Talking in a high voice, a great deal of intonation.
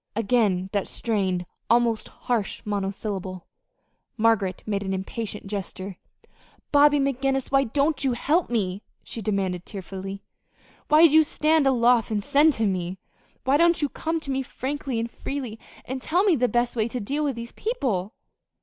Yes: high, 235 Hz; wide, 5.7 semitones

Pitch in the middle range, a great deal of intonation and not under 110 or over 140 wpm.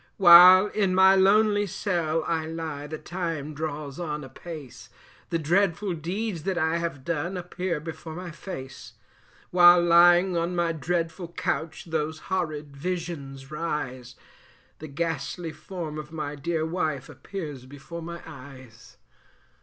No: medium, 165 Hz; average, 2.8 semitones; slow, 135 wpm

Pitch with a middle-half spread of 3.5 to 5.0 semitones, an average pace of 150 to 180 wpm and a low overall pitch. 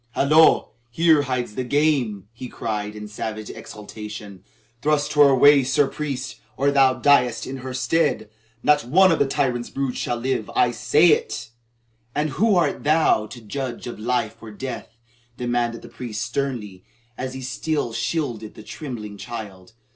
Yes: average, 4.4 semitones; average, 160 wpm; low, 125 Hz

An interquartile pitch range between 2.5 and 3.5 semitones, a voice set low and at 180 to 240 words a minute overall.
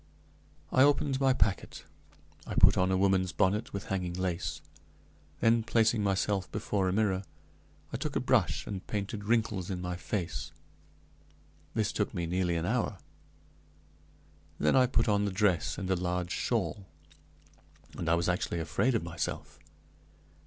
No: average, 3.1 semitones; very low, 95 Hz; average, 150 wpm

